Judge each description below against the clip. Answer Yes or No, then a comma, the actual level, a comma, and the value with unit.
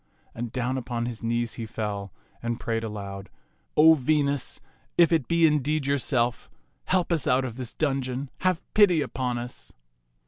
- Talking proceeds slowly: No, average, 165 wpm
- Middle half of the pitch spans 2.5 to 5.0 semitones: Yes, average, 4.4 semitones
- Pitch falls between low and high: No, low, 130 Hz